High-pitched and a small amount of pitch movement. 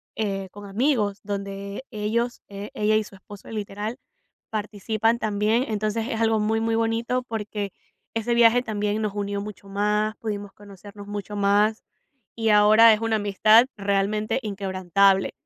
Yes: high, 210 Hz; narrow, 1.7 semitones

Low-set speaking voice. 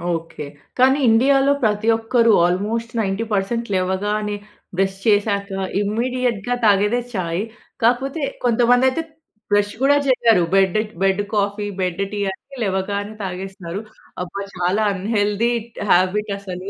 No: high, 205 Hz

